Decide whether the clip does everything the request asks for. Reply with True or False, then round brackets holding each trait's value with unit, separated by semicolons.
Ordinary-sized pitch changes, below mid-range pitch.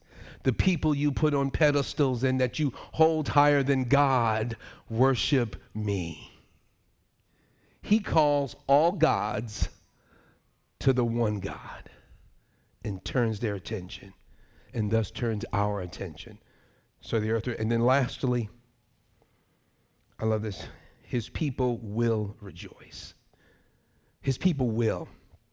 True (4.0 semitones; 115 Hz)